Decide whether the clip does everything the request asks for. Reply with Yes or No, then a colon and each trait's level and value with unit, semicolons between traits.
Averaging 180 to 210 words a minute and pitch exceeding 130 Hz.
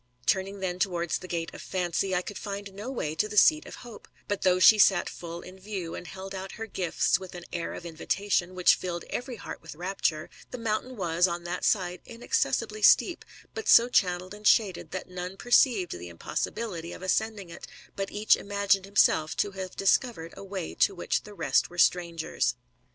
Yes: average, 200 wpm; high, 190 Hz